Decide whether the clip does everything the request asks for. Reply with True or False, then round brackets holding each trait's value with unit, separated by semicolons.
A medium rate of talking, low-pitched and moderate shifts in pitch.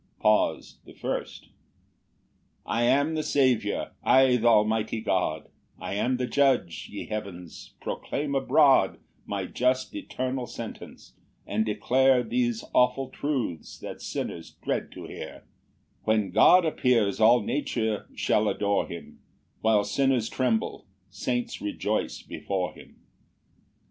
False (125 wpm; 120 Hz; 3.8 semitones)